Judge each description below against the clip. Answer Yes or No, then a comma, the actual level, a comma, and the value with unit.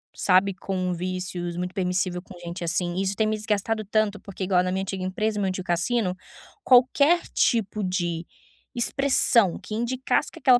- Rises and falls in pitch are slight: No, average, 3.1 semitones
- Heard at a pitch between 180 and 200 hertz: Yes, high, 190 Hz